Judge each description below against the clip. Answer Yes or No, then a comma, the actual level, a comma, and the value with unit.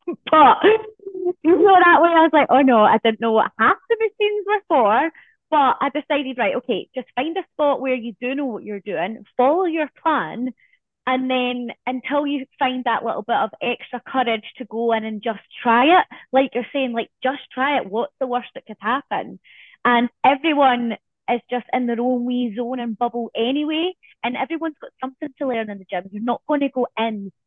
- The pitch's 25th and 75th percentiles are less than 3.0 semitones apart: No, average, 4.5 semitones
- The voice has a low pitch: No, very high, 255 Hz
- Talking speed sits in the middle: No, fast, 210 wpm